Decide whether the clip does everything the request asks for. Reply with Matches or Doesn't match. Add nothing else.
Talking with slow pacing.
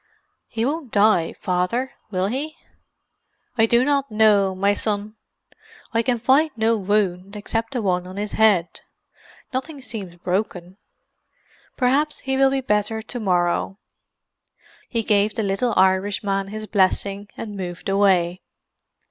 Matches